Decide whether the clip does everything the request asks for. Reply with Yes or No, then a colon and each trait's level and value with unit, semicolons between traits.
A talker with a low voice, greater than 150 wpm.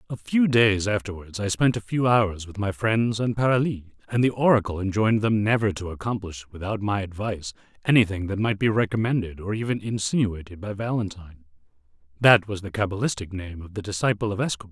Yes: low, 105 Hz; average, 185 wpm